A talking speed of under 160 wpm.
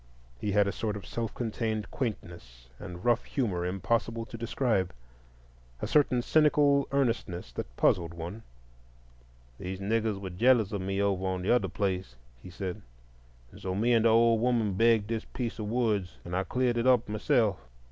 No: average, 175 wpm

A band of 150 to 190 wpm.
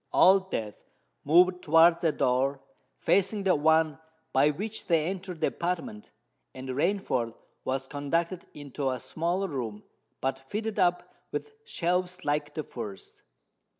No: slow, 135 wpm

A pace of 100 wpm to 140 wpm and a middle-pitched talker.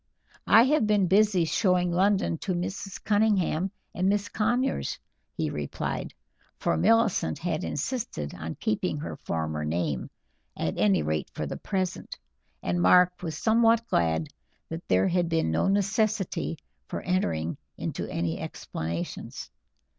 Yes: slow, 135 wpm; medium, 180 Hz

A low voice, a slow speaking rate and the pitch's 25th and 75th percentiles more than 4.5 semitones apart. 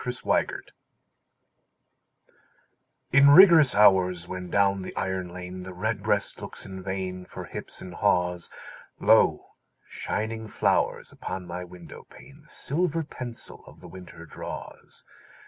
Yes: very low, 95 Hz; slow, 125 wpm; average, 5.1 semitones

